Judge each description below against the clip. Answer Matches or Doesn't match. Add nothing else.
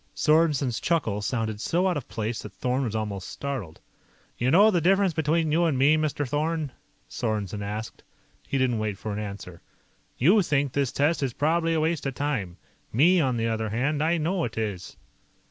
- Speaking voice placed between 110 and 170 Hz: Matches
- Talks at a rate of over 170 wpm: Matches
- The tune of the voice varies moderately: Doesn't match